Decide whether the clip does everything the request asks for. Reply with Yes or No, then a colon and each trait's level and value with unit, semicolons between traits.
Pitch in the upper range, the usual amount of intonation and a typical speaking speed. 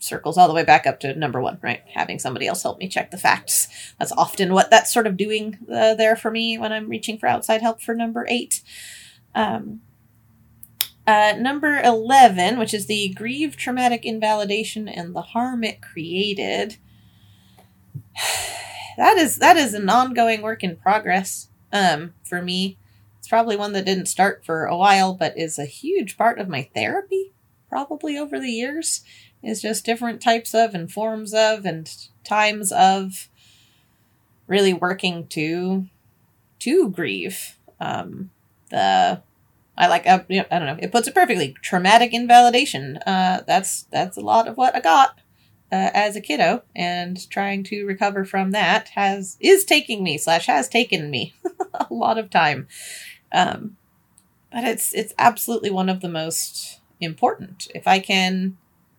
Yes: high, 205 Hz; average, 4.7 semitones; average, 165 wpm